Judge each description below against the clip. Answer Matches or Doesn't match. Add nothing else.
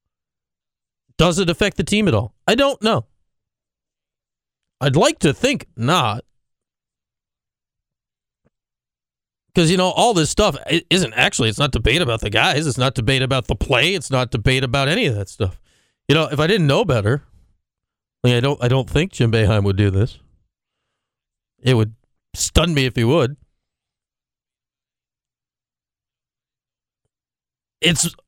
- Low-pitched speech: Matches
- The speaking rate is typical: Matches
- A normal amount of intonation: Doesn't match